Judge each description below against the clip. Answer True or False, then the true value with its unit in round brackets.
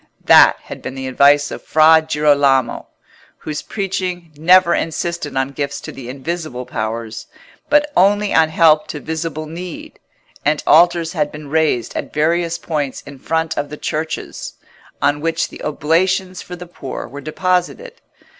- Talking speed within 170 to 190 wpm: False (155 wpm)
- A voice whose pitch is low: False (155 Hz)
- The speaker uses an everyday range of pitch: True (3.2 semitones)